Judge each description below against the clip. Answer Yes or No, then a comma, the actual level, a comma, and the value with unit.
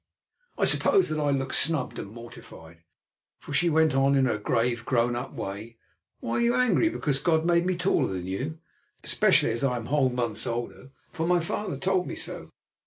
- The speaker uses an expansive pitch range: Yes, wide, 5.9 semitones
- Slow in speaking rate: No, average, 195 wpm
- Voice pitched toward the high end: No, low, 135 Hz